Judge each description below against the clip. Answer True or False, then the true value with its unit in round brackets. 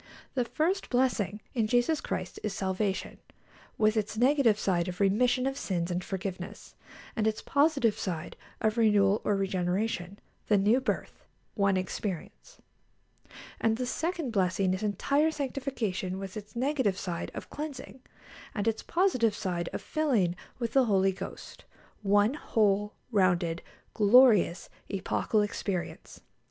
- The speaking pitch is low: False (210 Hz)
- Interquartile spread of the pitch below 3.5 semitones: False (4.7 semitones)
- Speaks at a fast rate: False (135 wpm)